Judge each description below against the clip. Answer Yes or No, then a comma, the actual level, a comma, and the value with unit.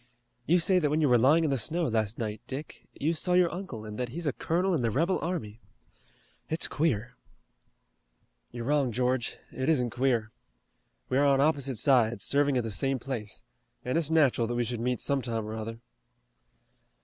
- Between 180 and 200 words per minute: Yes, average, 190 wpm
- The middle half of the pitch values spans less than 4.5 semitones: No, average, 5.0 semitones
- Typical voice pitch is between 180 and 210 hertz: No, low, 130 Hz